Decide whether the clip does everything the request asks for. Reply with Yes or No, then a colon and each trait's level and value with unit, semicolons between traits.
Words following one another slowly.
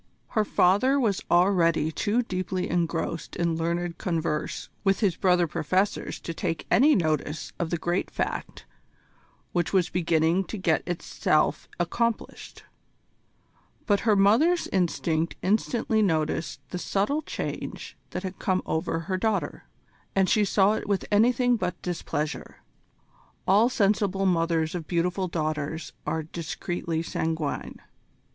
Yes: slow, 130 wpm